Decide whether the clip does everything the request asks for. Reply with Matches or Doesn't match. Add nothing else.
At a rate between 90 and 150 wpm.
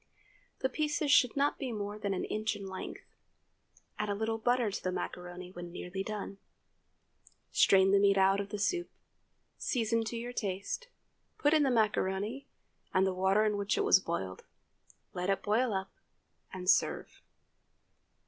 Doesn't match